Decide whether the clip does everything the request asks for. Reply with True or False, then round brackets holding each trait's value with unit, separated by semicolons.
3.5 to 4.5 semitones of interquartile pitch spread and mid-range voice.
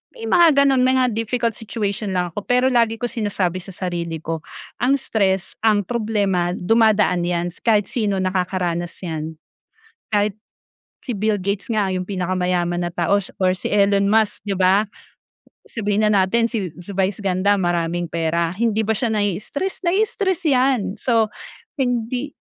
False (4.0 semitones; 205 Hz)